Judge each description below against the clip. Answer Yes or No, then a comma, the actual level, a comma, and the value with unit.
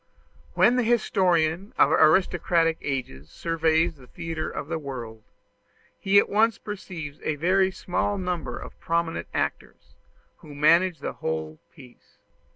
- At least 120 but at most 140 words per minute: Yes, slow, 135 wpm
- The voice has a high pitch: No, medium, 165 Hz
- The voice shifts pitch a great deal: No, average, 4.5 semitones